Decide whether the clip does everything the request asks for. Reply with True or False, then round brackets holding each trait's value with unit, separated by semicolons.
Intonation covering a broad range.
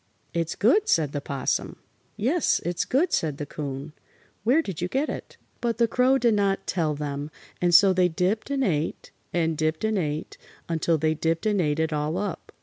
True (6.0 semitones)